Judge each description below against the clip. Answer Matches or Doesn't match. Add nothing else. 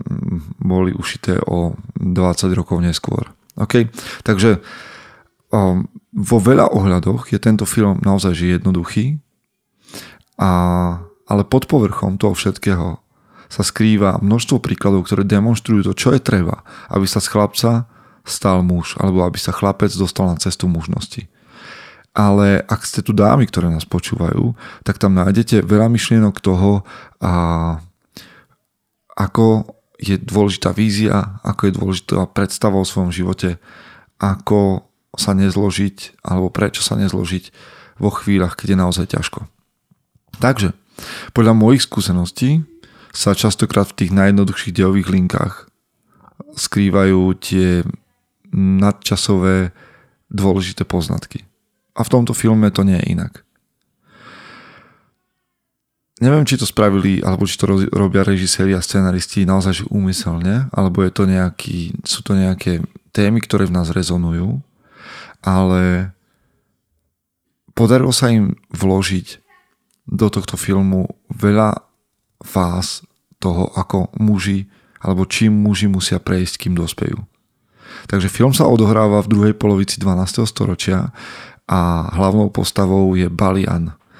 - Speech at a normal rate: Matches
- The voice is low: Matches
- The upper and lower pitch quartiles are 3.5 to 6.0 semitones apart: Doesn't match